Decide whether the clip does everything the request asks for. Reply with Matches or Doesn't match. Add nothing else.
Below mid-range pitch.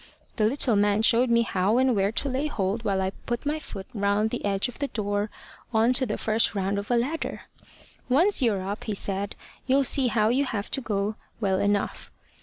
Doesn't match